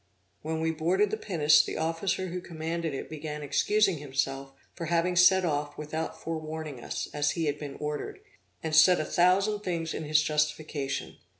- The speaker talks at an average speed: Yes, average, 175 wpm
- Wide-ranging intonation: No, average, 2.8 semitones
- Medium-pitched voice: Yes, medium, 160 Hz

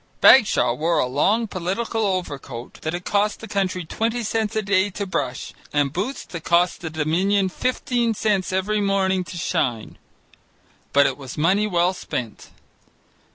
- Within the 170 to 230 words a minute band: No, average, 155 wpm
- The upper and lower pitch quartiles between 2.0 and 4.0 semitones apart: No, average, 4.7 semitones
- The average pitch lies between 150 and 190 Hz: Yes, medium, 185 Hz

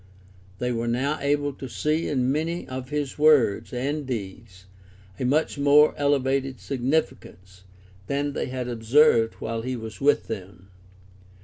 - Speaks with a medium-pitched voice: No, low, 130 Hz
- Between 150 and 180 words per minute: No, average, 140 wpm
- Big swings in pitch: No, average, 3.9 semitones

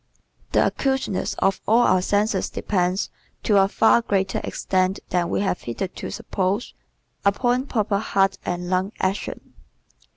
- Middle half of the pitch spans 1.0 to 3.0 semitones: Yes, narrow, 2.5 semitones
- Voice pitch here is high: Yes, high, 195 Hz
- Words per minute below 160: Yes, slow, 135 wpm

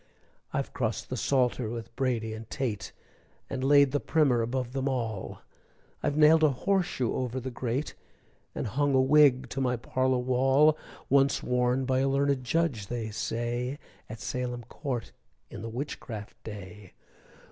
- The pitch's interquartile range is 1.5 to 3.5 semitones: Yes, average, 2.7 semitones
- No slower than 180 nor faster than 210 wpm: No, average, 155 wpm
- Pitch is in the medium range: No, low, 130 Hz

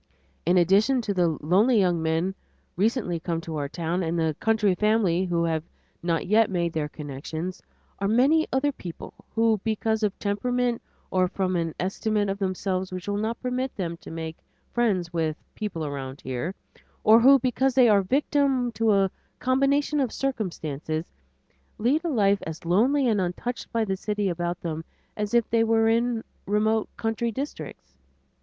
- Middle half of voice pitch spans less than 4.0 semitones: No, average, 5.2 semitones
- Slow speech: No, average, 170 wpm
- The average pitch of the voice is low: No, high, 200 Hz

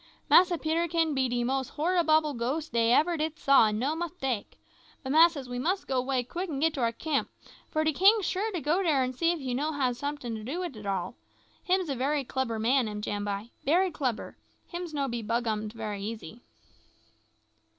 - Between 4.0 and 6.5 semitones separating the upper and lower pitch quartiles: Yes, average, 5.3 semitones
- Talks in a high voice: Yes, very high, 275 Hz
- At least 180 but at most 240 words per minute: Yes, average, 200 wpm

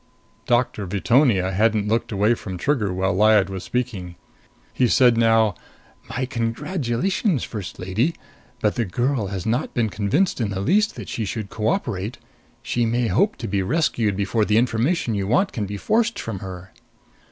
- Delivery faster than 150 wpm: Yes, average, 165 wpm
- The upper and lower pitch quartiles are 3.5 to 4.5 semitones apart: Yes, average, 3.9 semitones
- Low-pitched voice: Yes, low, 110 Hz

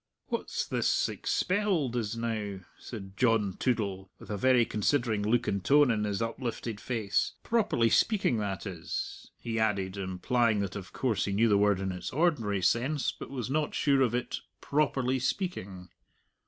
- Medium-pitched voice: No, low, 115 Hz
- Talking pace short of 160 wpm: No, average, 165 wpm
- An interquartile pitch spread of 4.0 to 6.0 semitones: Yes, average, 4.4 semitones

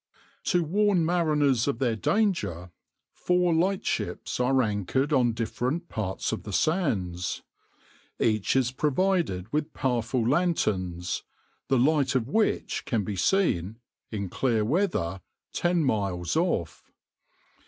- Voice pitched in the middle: No, low, 130 Hz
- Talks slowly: Yes, slow, 120 wpm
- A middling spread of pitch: No, wide, 8.2 semitones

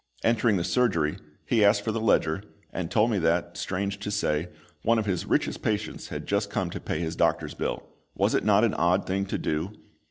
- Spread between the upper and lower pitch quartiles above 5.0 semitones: No, average, 3.6 semitones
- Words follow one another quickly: Yes, fast, 215 wpm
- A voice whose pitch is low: Yes, low, 100 Hz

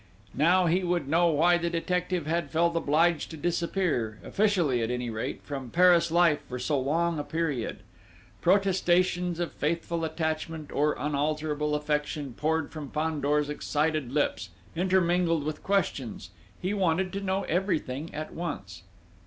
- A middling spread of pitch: Yes, average, 3.0 semitones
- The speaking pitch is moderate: Yes, medium, 160 Hz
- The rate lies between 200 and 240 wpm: No, average, 145 wpm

